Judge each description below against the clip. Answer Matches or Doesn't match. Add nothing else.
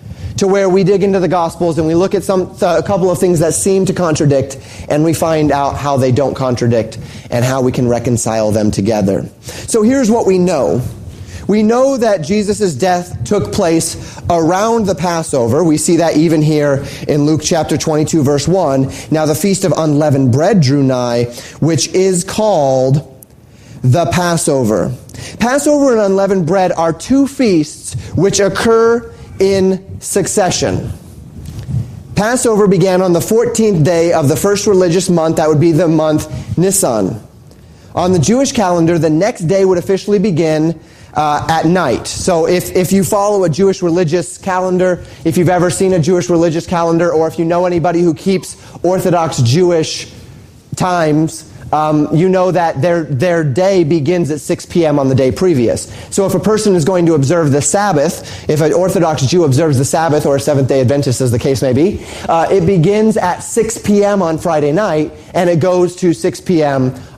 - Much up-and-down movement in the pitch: Doesn't match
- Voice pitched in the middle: Matches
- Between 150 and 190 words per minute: Matches